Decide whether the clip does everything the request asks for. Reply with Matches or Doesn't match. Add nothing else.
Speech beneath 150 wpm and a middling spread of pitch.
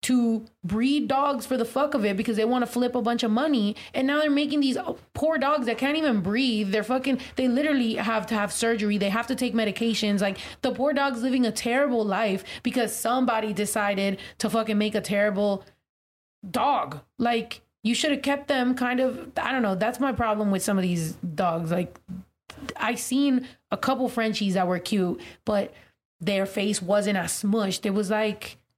Doesn't match